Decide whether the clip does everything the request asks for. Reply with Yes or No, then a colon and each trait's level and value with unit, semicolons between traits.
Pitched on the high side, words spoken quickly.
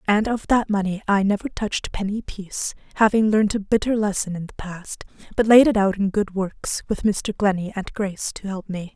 Yes: high, 205 Hz; fast, 215 wpm